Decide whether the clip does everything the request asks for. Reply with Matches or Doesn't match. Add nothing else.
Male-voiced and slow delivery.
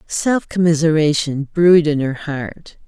Doesn't match